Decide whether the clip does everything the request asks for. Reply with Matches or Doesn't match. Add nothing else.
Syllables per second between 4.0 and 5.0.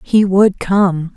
Doesn't match